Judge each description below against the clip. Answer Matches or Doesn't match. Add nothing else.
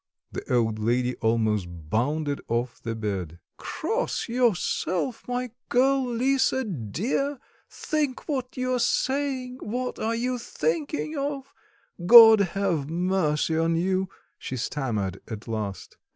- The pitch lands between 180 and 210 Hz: Matches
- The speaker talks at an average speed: Doesn't match